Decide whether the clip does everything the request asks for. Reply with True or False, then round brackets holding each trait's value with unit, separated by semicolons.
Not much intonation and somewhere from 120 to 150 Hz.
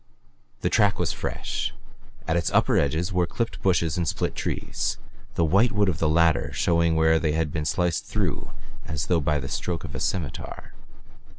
False (2.3 semitones; 85 Hz)